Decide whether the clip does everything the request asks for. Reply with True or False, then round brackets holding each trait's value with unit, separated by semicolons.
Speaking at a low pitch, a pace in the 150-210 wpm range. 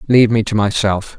True (110 Hz; 200 wpm)